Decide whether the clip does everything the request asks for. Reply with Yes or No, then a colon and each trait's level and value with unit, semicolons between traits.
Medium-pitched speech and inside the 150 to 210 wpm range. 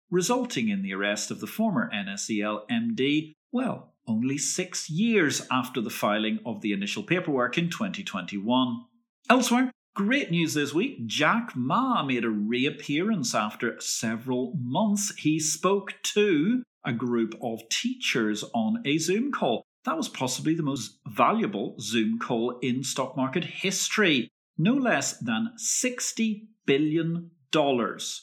No: medium, 165 Hz; slow, 135 wpm